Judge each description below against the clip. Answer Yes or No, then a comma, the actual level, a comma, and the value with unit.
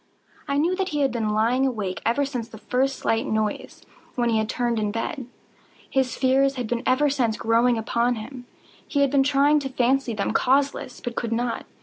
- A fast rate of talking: Yes, fast, 210 wpm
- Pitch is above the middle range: Yes, very high, 250 Hz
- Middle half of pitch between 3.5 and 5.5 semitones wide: No, average, 3.1 semitones